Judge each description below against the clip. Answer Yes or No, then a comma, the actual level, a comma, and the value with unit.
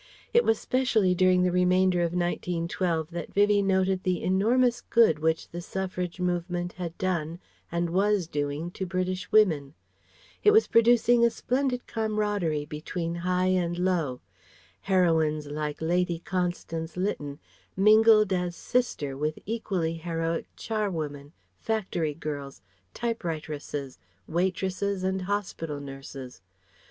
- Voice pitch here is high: No, medium, 180 Hz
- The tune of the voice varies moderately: Yes, average, 3.5 semitones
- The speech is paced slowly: Yes, slow, 125 wpm